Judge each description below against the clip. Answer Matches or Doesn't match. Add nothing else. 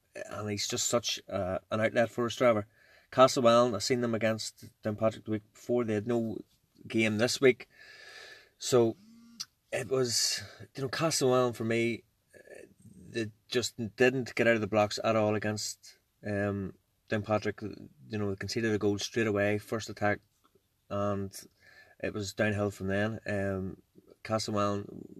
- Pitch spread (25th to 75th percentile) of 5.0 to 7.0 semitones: Doesn't match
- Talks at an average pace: Matches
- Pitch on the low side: Matches